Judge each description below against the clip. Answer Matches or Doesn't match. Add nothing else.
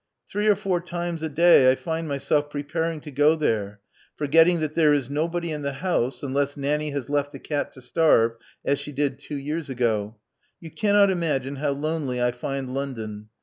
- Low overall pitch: Doesn't match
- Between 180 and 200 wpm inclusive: Matches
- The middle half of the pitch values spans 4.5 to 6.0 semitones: Doesn't match